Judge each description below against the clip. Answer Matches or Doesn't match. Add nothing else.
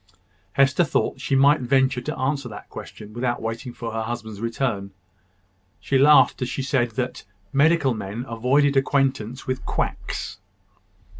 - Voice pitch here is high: Doesn't match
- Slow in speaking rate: Doesn't match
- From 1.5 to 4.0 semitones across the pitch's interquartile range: Matches